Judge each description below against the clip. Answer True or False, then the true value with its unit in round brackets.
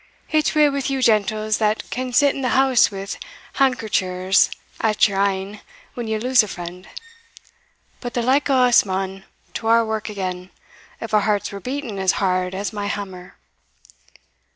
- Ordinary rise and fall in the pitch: True (4.5 semitones)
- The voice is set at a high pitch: True (215 Hz)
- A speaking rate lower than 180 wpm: True (170 wpm)